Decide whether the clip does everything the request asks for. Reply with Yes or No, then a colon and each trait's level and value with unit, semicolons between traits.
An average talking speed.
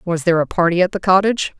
No: fast, 265 wpm